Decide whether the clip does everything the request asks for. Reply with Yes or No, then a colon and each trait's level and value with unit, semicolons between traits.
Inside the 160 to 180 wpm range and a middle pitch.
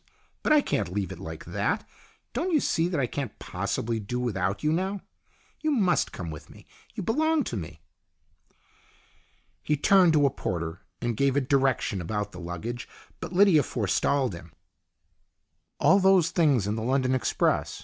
No: average, 170 wpm; low, 130 Hz